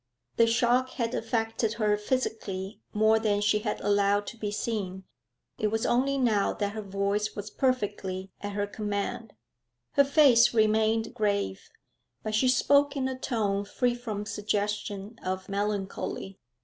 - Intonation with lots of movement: No, narrow, 2.4 semitones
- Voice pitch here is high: Yes, high, 215 Hz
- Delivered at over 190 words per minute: No, average, 150 wpm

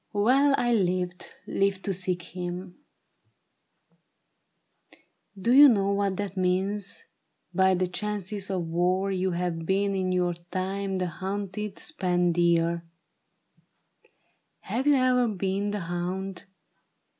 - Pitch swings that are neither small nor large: No, narrow, 2.2 semitones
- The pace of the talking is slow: Yes, slow, 120 wpm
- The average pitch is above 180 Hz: Yes, high, 190 Hz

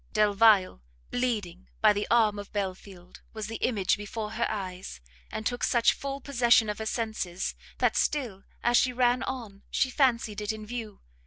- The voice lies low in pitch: No, high, 220 Hz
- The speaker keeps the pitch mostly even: No, average, 3.0 semitones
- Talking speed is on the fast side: No, average, 170 wpm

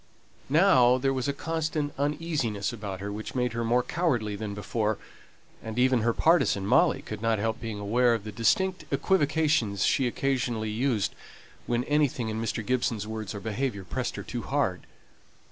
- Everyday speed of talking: Yes, average, 170 wpm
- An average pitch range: Yes, average, 4.3 semitones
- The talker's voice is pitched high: No, low, 120 Hz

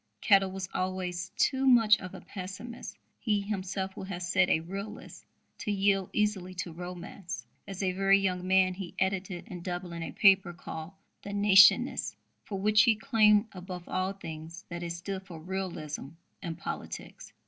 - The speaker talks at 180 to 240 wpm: No, average, 165 wpm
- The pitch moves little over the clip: Yes, narrow, 2.0 semitones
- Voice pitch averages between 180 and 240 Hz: Yes, high, 190 Hz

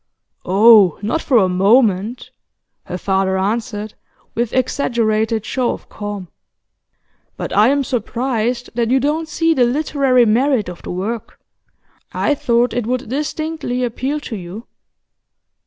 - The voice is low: No, high, 235 Hz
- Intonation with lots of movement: No, average, 3.9 semitones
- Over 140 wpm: No, slow, 135 wpm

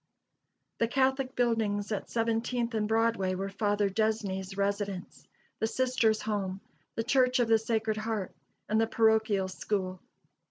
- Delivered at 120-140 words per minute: Yes, slow, 135 wpm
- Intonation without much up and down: Yes, narrow, 2.3 semitones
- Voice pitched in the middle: No, high, 220 Hz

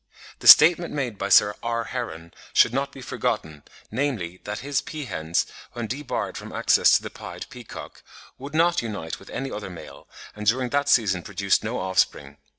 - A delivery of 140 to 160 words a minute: No, average, 175 wpm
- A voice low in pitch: Yes, low, 115 Hz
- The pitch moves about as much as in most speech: No, wide, 6.5 semitones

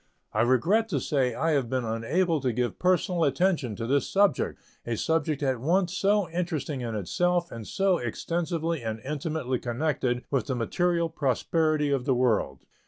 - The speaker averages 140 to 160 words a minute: No, average, 170 wpm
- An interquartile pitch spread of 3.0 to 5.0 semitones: No, wide, 5.6 semitones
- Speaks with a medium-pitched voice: Yes, medium, 145 Hz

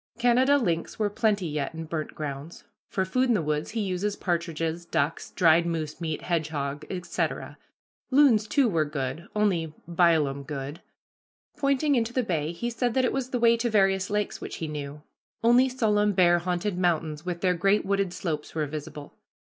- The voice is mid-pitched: Yes, medium, 175 Hz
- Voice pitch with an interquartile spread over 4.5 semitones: Yes, wide, 5.6 semitones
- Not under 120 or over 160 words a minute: No, average, 180 wpm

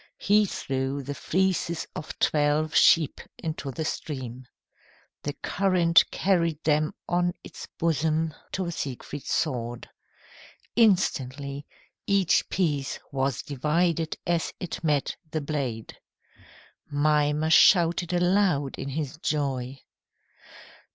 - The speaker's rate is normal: No, slow, 105 wpm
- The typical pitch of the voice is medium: Yes, medium, 155 Hz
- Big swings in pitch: No, average, 3.6 semitones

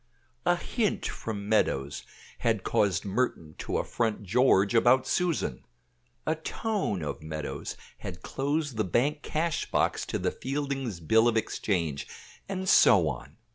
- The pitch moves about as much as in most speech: No, wide, 7.6 semitones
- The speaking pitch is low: Yes, low, 115 Hz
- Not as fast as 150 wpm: Yes, slow, 135 wpm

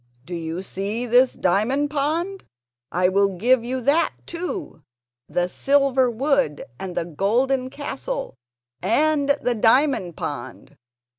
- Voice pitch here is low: No, high, 245 Hz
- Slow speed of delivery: Yes, slow, 125 wpm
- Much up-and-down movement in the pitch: Yes, wide, 7.0 semitones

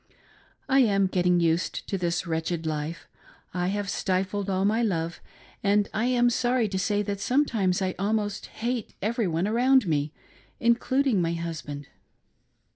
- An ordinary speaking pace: Yes, average, 150 wpm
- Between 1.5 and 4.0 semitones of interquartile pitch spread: No, average, 4.7 semitones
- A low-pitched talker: No, high, 195 Hz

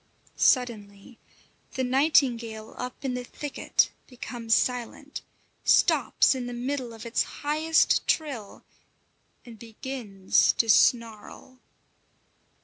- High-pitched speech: Yes, high, 245 Hz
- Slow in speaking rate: Yes, slow, 100 wpm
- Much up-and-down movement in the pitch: No, average, 2.7 semitones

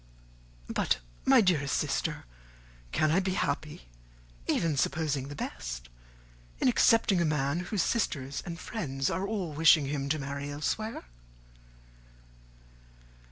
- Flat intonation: No, average, 4.8 semitones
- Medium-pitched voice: Yes, medium, 155 Hz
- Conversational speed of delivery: No, slow, 120 wpm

